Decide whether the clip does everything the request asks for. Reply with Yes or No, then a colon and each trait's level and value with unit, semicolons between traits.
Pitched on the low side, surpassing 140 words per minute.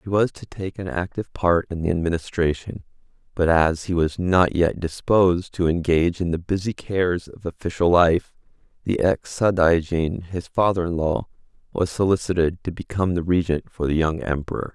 Yes: very low, 85 Hz; average, 175 wpm